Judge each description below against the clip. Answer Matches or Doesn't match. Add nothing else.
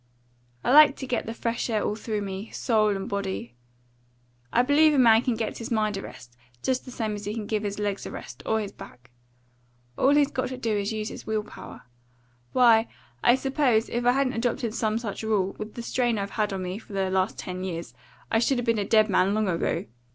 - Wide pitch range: Doesn't match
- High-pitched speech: Matches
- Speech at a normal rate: Doesn't match